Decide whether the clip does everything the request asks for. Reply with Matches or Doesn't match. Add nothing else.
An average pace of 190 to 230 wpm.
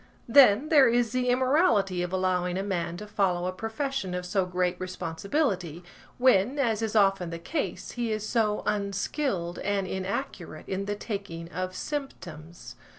Doesn't match